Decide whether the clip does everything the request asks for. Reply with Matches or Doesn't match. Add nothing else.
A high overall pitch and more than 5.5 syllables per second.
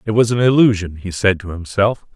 Doesn't match